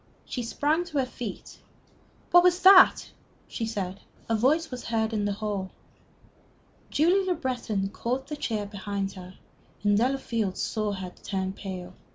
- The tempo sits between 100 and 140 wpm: No, average, 155 wpm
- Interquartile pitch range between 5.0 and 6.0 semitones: Yes, wide, 5.4 semitones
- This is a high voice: Yes, high, 220 Hz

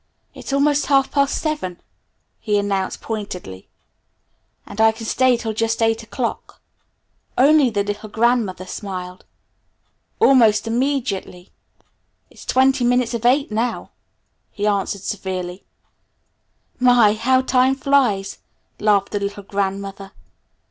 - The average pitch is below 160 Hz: No, high, 220 Hz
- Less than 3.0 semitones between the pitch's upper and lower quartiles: No, average, 4.2 semitones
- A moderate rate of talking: No, slow, 115 wpm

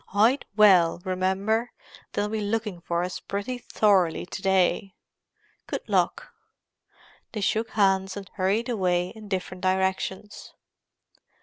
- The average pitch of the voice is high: Yes, high, 195 Hz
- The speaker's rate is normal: No, slow, 120 wpm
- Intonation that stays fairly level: Yes, narrow, 2.3 semitones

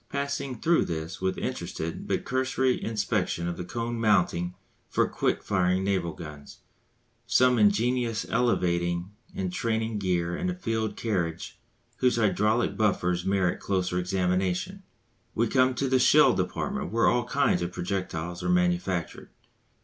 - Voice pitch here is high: No, low, 100 Hz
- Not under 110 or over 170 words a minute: Yes, average, 140 wpm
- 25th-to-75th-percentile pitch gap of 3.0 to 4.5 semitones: No, average, 5.3 semitones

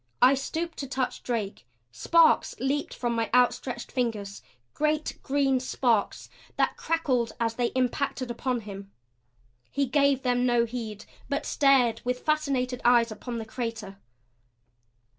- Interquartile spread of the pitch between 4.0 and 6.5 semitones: No, average, 3.0 semitones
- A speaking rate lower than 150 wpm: Yes, slow, 135 wpm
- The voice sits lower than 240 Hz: No, very high, 250 Hz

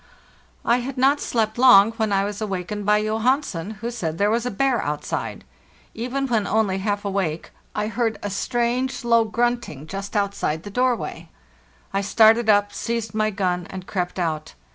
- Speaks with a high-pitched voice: Yes, high, 215 Hz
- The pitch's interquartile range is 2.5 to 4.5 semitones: Yes, average, 3.3 semitones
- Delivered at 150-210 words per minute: Yes, average, 175 wpm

